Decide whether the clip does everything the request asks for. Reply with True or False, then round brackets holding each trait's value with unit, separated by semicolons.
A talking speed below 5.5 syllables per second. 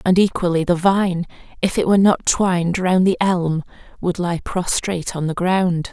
True (4.8 syllables/s)